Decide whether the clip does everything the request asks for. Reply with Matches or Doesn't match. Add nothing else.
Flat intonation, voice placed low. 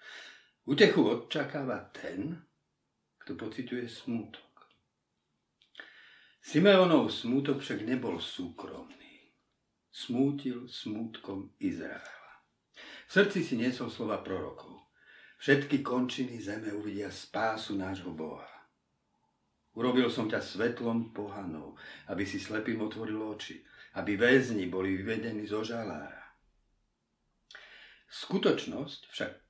Doesn't match